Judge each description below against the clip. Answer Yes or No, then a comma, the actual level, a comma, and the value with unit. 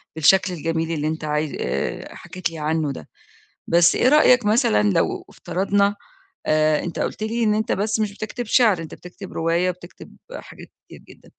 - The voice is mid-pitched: Yes, medium, 175 Hz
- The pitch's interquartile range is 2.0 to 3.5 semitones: No, average, 5.0 semitones